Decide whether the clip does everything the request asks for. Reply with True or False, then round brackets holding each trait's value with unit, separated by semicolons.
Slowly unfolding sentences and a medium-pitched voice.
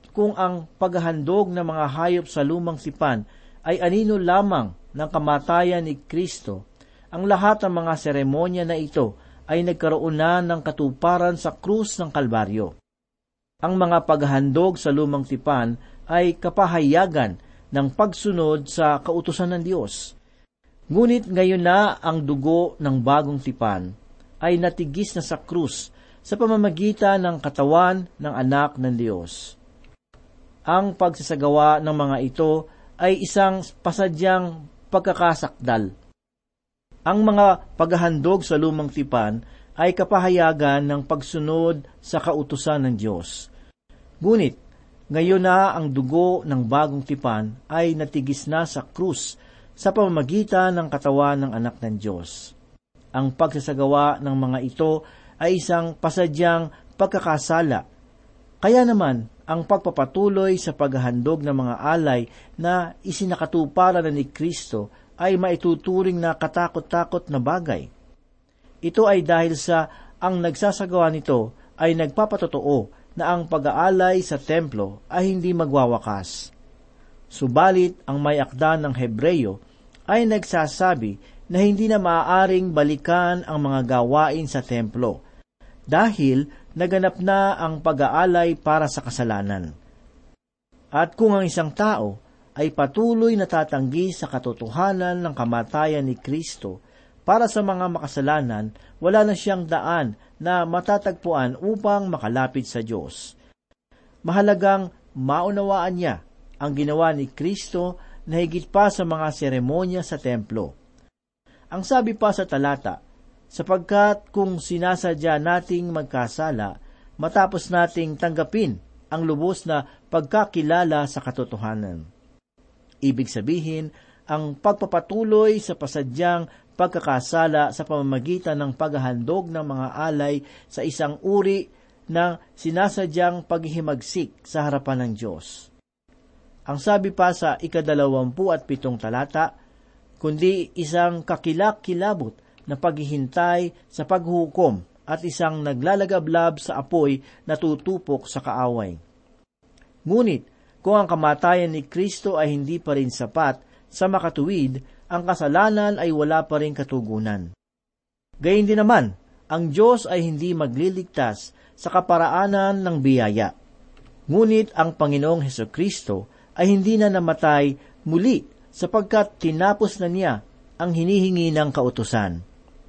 False (120 wpm; 160 Hz)